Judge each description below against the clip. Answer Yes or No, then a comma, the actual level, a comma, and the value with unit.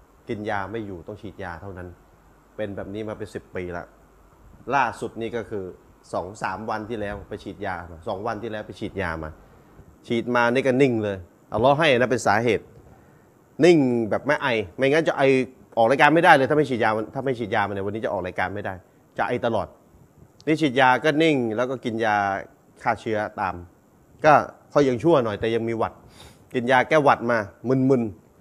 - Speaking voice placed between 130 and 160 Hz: No, low, 110 Hz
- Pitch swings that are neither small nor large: Yes, average, 4.3 semitones